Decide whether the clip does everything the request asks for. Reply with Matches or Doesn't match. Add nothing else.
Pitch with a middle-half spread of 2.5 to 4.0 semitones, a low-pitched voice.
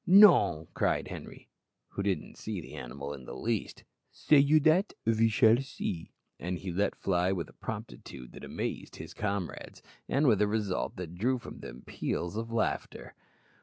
Doesn't match